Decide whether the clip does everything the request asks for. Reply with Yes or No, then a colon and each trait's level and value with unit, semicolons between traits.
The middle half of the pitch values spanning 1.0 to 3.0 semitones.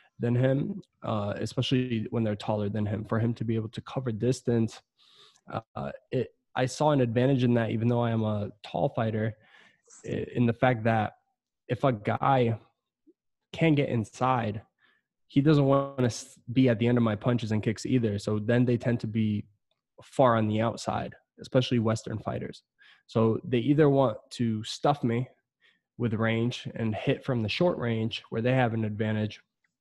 Yes: narrow, 2.6 semitones